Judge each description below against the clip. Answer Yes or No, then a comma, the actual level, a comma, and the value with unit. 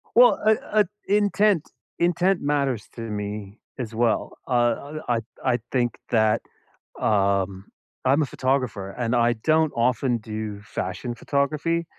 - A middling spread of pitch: No, wide, 5.9 semitones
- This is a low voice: Yes, low, 120 Hz